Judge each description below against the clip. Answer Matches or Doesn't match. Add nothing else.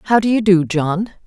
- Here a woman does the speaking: Matches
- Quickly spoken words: Matches